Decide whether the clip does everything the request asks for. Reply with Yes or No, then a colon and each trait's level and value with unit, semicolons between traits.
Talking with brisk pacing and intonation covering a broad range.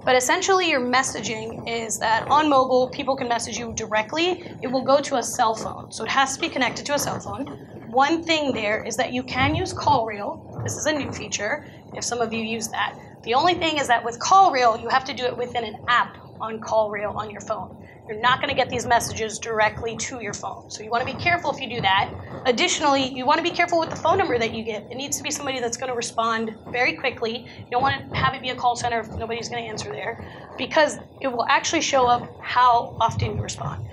No: fast, 255 wpm; average, 3.6 semitones